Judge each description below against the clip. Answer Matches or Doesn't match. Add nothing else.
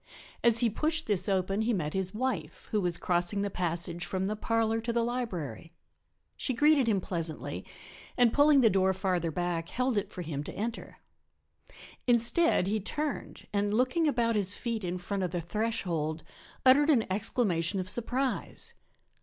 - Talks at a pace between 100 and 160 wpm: Doesn't match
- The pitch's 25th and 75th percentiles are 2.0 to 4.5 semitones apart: Doesn't match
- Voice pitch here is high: Matches